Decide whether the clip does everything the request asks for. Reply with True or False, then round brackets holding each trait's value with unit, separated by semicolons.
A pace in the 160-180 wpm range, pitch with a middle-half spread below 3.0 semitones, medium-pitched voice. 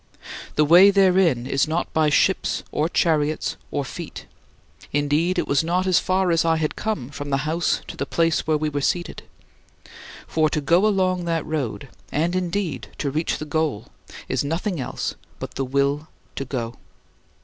False (175 wpm; 3.4 semitones; 155 Hz)